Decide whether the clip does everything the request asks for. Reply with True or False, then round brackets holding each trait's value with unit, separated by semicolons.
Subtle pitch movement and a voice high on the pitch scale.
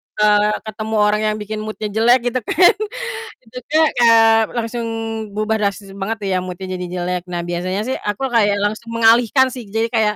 True (2.1 semitones; 215 Hz)